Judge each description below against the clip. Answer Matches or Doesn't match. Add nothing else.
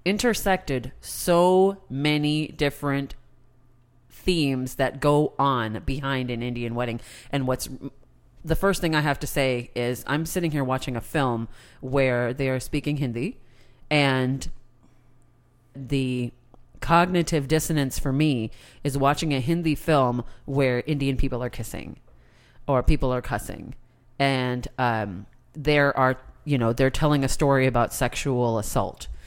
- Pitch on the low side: Matches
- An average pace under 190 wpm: Matches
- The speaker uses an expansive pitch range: Doesn't match